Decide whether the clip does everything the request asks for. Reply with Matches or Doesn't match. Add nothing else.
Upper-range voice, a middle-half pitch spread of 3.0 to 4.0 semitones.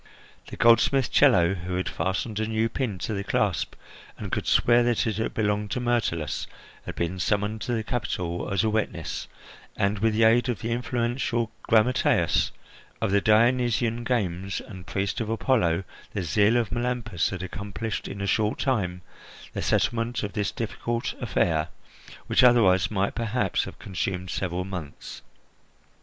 Doesn't match